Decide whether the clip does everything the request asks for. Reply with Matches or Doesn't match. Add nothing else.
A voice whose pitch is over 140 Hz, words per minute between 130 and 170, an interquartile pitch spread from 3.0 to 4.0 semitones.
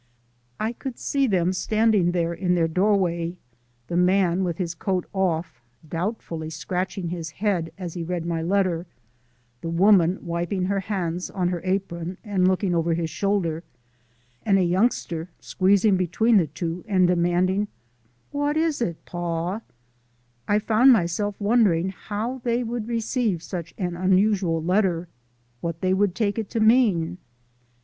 Matches